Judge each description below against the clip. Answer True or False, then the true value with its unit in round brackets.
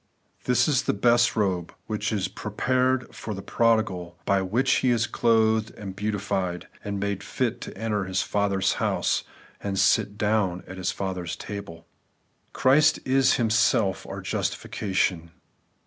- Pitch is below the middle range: True (105 Hz)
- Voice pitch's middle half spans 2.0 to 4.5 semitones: True (3.3 semitones)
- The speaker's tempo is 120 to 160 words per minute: True (150 wpm)